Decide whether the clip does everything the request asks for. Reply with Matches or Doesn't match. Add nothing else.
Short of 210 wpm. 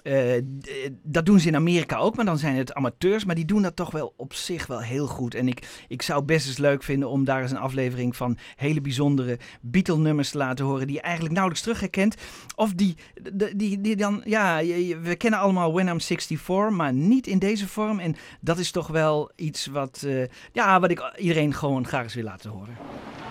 Doesn't match